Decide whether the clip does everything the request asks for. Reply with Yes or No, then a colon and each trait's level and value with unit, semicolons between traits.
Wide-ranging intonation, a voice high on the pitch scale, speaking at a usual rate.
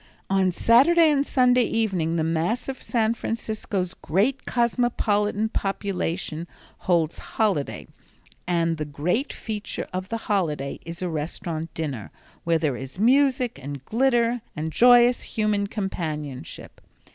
No: wide, 6.2 semitones; high, 195 Hz; slow, 125 wpm